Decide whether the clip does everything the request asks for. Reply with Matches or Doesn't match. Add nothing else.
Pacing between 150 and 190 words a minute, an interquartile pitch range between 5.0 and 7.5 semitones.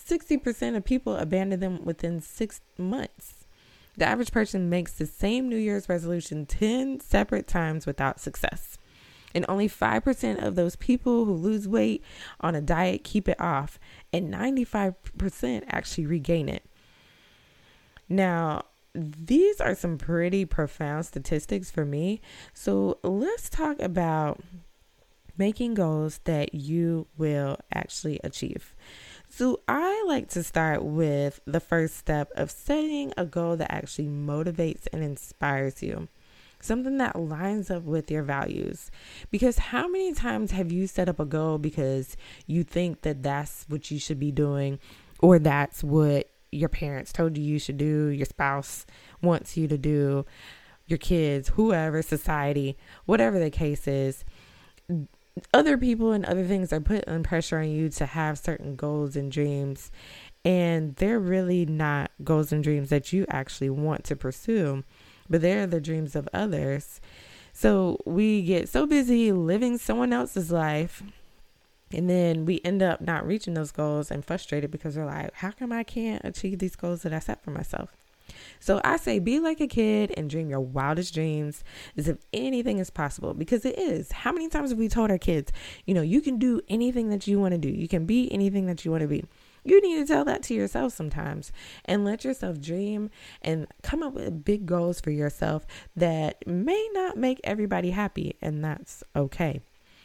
Matches